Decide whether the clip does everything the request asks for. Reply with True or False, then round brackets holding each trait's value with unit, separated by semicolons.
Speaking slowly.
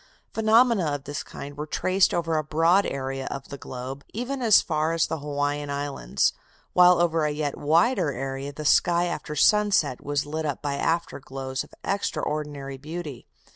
False (175 wpm)